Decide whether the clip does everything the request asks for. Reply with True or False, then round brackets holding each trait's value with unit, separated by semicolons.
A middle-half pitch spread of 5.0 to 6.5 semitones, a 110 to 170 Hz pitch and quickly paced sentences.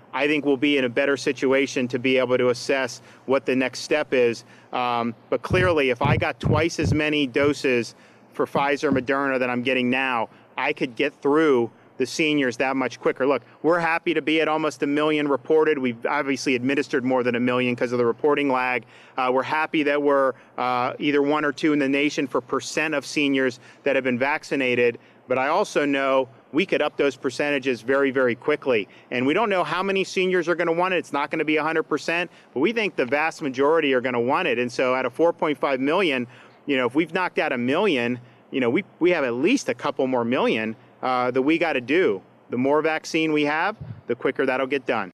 False (3.2 semitones; 135 Hz; 225 wpm)